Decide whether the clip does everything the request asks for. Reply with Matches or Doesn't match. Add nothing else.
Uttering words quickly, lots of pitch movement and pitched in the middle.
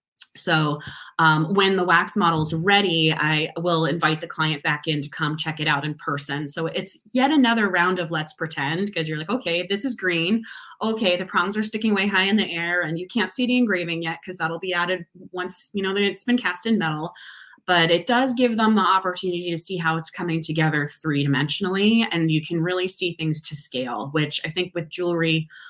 Doesn't match